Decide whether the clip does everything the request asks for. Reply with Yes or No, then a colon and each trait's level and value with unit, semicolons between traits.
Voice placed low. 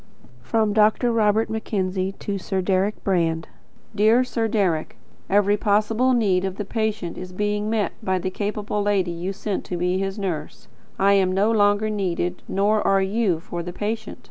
No: high, 200 Hz